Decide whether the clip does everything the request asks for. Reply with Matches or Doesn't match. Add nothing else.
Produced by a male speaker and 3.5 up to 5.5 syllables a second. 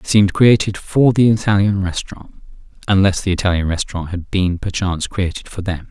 Doesn't match